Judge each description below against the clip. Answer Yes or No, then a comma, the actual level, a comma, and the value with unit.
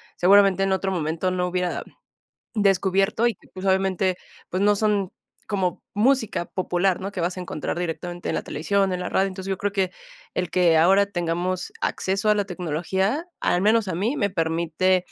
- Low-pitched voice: No, high, 190 Hz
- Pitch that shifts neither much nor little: No, narrow, 2.0 semitones